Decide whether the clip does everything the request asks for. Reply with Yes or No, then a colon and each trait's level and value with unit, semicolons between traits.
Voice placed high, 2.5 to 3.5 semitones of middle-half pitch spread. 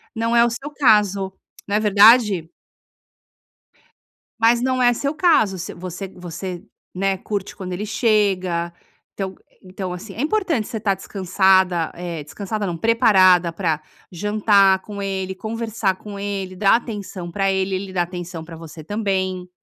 Yes: high, 195 Hz; average, 2.9 semitones